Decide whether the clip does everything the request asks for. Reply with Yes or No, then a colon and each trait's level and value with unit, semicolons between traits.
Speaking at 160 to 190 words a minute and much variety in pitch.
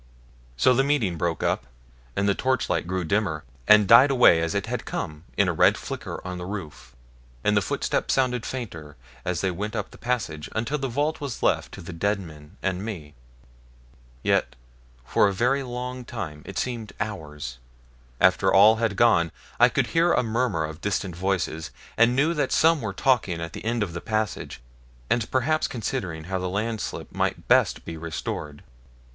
Yes: average, 185 wpm; wide, 6.3 semitones